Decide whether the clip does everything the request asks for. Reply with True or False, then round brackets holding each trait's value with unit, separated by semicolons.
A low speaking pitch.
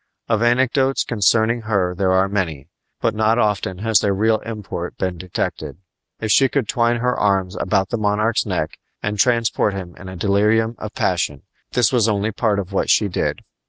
True (105 Hz)